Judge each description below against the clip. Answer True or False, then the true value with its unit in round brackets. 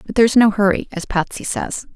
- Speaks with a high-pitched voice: True (210 Hz)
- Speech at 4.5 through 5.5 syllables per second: False (5.8 syllables/s)